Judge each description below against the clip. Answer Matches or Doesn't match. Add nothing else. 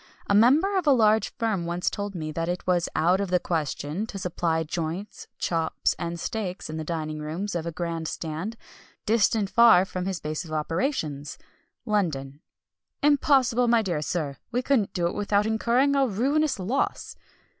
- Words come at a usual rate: Matches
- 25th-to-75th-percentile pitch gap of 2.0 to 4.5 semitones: Doesn't match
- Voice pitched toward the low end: Doesn't match